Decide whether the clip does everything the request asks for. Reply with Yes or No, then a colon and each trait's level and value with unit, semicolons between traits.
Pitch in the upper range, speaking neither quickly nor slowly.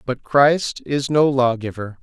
No: low, 130 Hz; average, 180 wpm